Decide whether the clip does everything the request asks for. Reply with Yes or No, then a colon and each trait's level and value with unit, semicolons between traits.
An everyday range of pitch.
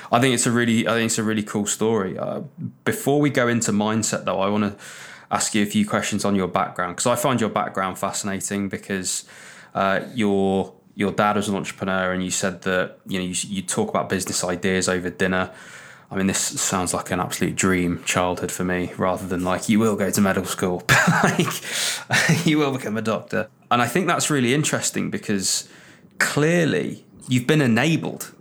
Yes: average, 4.0 semitones